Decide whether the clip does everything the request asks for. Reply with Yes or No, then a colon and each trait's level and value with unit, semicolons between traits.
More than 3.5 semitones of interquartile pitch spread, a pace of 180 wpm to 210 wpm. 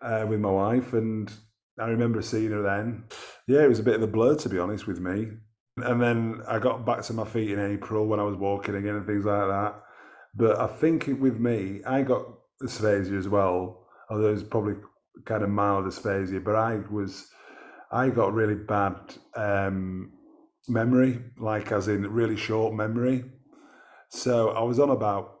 No: narrow, 2.5 semitones; average, 190 wpm